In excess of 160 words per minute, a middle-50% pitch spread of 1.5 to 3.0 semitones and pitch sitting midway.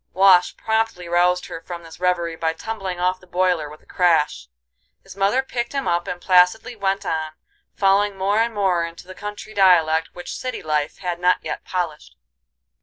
Yes: average, 180 wpm; average, 2.7 semitones; medium, 180 Hz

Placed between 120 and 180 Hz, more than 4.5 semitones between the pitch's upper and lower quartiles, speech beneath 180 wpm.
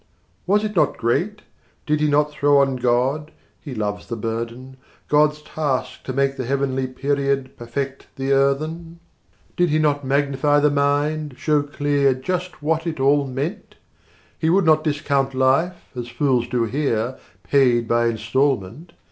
No: medium, 140 Hz; narrow, 2.6 semitones; average, 155 wpm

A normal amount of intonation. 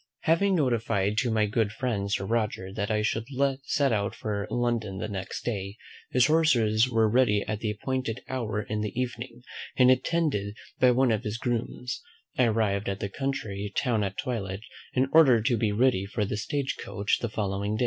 Yes: average, 3.6 semitones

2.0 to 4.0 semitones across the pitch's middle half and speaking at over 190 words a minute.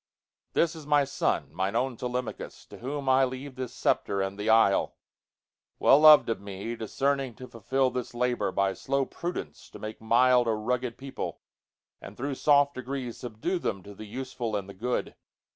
No: average, 3.7 semitones; average, 160 wpm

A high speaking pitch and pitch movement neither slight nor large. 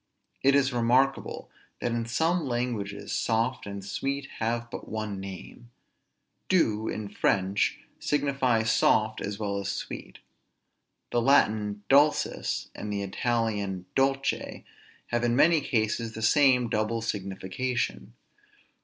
No: low, 115 Hz; average, 4.1 semitones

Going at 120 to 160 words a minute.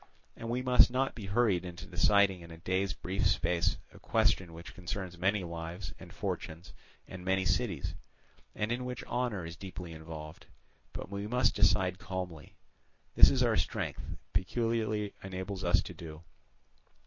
Yes: average, 150 wpm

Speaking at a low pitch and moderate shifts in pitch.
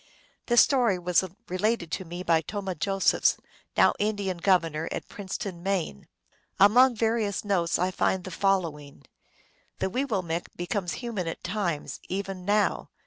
No: high, 190 Hz; average, 3.0 semitones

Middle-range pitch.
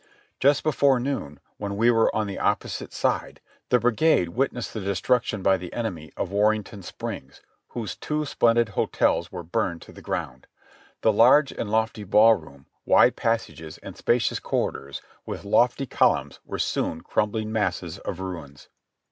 No: low, 110 Hz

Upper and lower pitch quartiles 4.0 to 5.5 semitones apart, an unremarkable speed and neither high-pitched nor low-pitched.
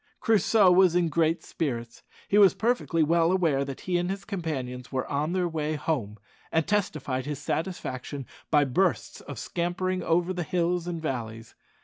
Yes: average, 4.4 semitones; average, 165 wpm; medium, 165 Hz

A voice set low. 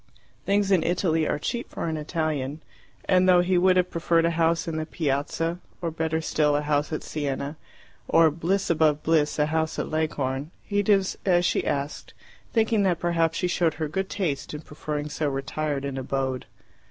No: medium, 160 Hz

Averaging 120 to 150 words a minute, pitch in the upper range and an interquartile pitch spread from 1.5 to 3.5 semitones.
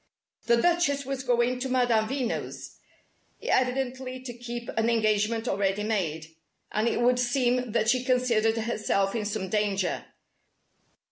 Yes: slow, 135 wpm; high, 235 Hz; average, 2.9 semitones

